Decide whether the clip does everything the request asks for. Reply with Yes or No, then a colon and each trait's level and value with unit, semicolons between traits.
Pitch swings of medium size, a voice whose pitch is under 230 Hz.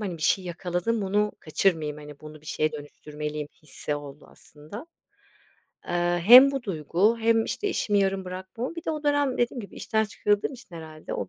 No: wide, 6.7 semitones; high, 190 Hz